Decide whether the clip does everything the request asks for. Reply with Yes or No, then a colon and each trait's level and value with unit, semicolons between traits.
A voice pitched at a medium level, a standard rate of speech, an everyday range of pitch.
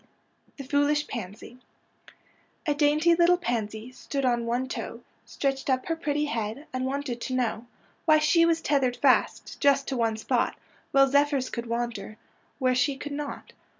No: very high, 270 Hz; average, 160 wpm; average, 3.5 semitones